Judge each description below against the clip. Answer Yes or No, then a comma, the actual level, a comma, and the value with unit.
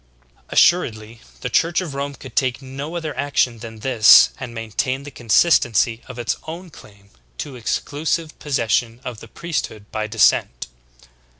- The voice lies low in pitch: Yes, low, 125 Hz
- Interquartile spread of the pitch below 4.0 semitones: No, average, 4.6 semitones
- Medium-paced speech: Yes, average, 155 wpm